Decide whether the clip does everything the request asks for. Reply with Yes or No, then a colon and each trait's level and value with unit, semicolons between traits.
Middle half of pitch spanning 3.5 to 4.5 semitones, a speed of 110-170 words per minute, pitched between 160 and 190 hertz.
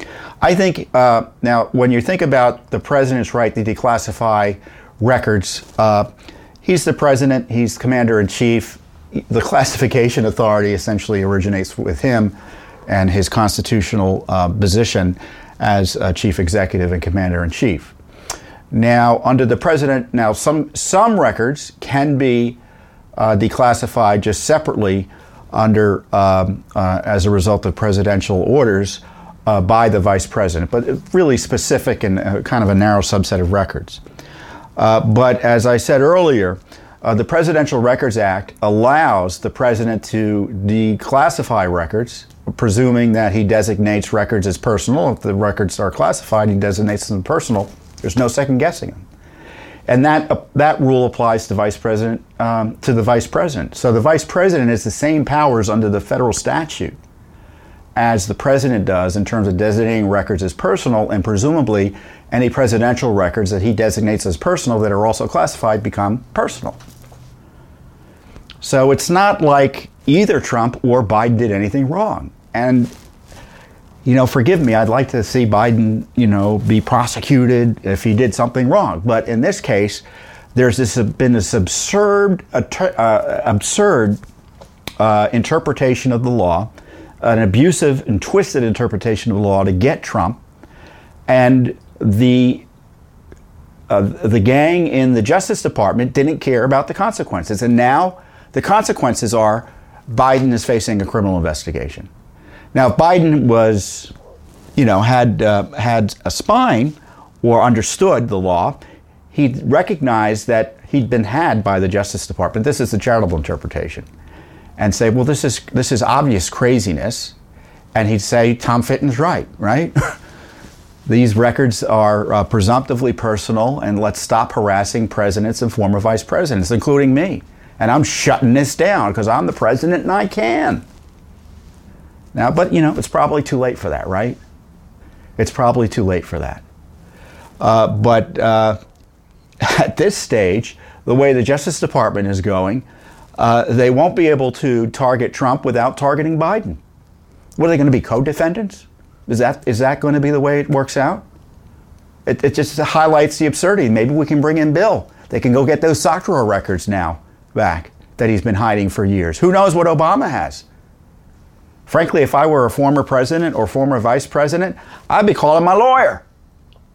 No: average, 4.2 semitones; average, 155 wpm; low, 115 Hz